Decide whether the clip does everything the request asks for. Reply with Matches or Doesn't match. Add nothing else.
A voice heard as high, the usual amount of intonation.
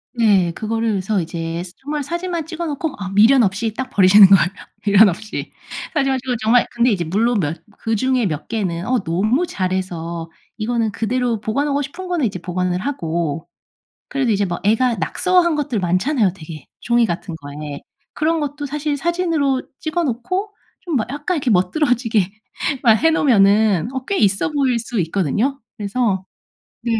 Doesn't match